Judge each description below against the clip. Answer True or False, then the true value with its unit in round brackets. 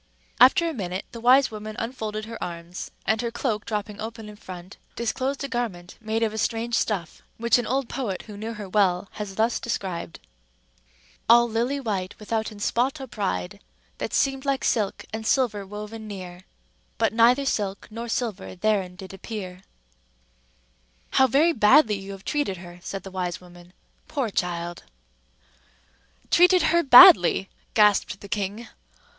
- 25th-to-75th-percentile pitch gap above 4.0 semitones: False (3.7 semitones)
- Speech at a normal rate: True (160 wpm)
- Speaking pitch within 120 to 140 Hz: False (215 Hz)